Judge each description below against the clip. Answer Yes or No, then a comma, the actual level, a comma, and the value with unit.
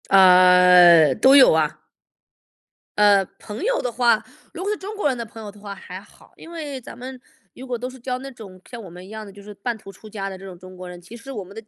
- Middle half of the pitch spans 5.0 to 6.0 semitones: Yes, average, 5.3 semitones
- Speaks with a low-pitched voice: No, high, 210 Hz